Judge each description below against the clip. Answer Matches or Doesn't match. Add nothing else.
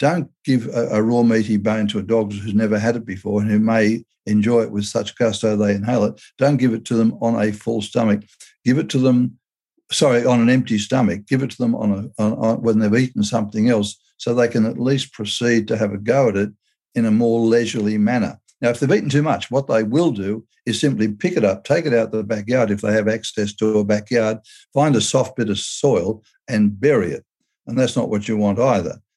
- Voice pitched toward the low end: Matches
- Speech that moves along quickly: Matches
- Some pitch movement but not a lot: Doesn't match